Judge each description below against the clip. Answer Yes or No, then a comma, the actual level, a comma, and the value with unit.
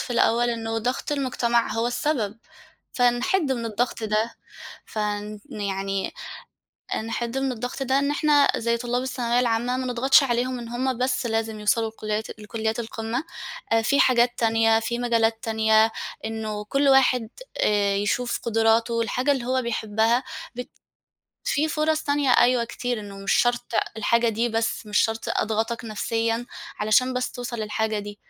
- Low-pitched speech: No, high, 235 Hz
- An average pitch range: No, narrow, 2.2 semitones